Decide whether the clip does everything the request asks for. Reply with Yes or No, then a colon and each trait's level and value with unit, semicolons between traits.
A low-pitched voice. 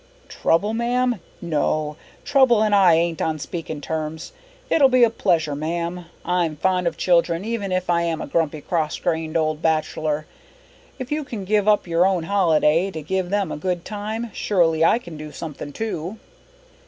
No: medium, 175 Hz